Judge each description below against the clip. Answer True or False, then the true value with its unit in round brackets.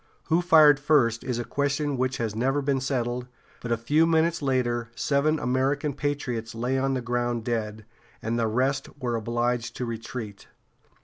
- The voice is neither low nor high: False (125 Hz)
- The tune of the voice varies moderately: True (3.3 semitones)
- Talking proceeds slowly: False (170 wpm)